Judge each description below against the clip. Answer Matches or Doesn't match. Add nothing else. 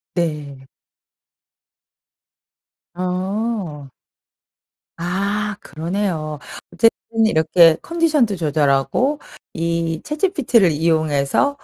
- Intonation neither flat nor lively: Doesn't match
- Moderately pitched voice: Matches